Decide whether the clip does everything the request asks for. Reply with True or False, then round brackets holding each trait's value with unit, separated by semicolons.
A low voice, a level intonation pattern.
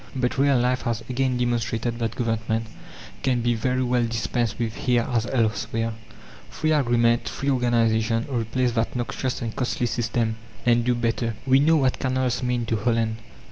True (120 Hz; 1.7 semitones)